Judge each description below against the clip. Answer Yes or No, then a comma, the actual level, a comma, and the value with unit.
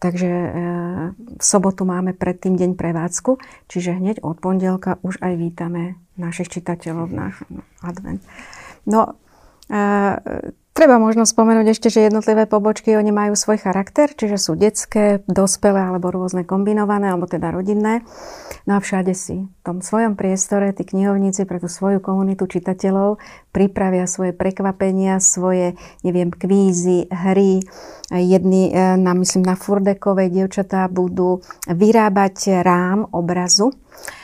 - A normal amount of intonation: No, narrow, 2.3 semitones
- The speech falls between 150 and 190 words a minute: No, average, 130 wpm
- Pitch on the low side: No, high, 190 Hz